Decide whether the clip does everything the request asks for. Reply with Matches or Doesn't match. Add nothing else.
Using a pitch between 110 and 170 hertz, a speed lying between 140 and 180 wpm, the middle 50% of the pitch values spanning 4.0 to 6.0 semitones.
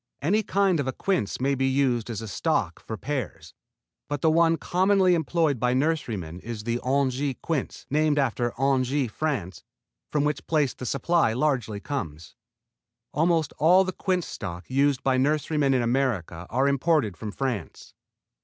Matches